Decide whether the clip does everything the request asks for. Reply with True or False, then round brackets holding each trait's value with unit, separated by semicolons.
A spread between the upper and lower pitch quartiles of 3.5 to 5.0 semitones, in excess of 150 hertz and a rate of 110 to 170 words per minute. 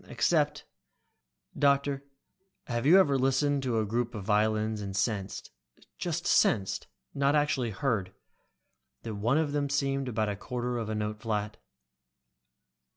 False (4.6 semitones; 120 Hz; 140 wpm)